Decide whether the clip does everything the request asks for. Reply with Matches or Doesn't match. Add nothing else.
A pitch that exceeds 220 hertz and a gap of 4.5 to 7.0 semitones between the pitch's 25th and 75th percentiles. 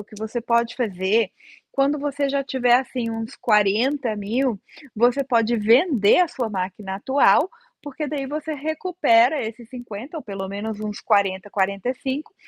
Matches